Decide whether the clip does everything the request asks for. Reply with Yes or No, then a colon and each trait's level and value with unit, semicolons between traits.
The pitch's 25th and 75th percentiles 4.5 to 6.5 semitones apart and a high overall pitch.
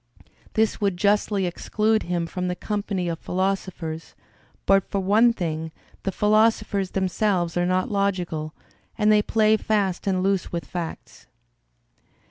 No: average, 3.0 semitones; high, 195 Hz